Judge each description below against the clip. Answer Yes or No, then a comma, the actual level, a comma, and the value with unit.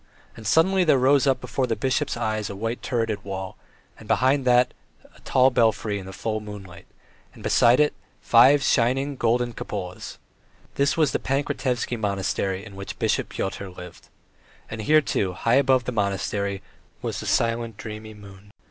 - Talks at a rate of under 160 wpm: No, average, 165 wpm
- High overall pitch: No, low, 115 Hz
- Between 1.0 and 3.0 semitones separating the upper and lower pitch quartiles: No, average, 4.4 semitones